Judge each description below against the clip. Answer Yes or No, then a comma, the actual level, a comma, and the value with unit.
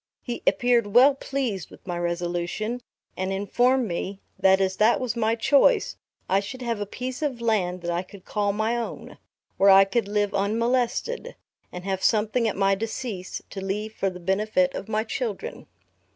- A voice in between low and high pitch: No, high, 210 Hz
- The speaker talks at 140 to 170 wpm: No, average, 180 wpm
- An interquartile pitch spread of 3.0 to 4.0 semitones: Yes, average, 3.7 semitones